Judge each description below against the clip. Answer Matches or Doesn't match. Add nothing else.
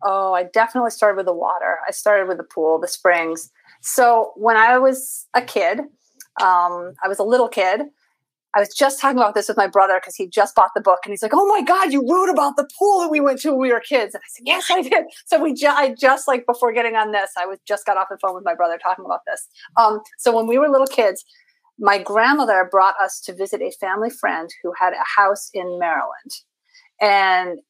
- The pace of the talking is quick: Matches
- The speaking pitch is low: Doesn't match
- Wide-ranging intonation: Matches